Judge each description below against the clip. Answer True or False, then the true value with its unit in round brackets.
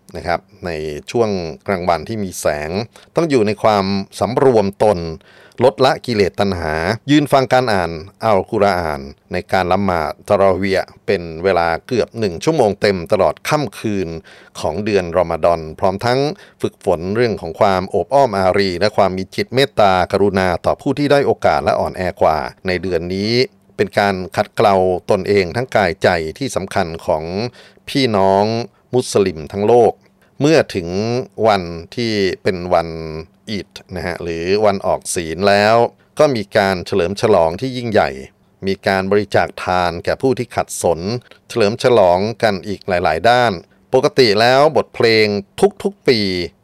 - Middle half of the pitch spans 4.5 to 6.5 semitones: False (3.7 semitones)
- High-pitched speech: False (100 Hz)